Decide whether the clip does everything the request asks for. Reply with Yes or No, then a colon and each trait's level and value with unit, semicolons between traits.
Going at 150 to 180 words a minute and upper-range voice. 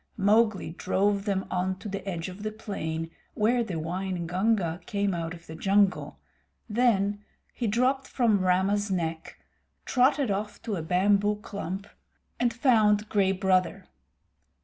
No: average, 140 wpm; high, 200 Hz